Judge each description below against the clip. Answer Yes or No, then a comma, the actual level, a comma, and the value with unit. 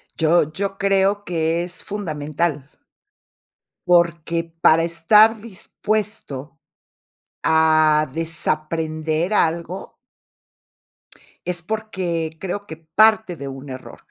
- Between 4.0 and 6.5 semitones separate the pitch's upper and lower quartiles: No, average, 3.6 semitones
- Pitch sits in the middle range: Yes, medium, 165 Hz